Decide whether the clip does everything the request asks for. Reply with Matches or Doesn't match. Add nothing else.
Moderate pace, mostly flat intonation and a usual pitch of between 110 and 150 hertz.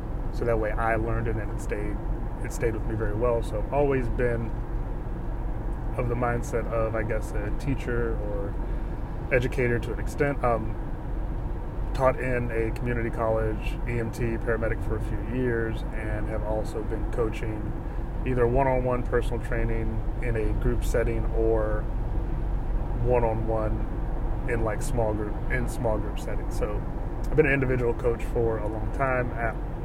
Matches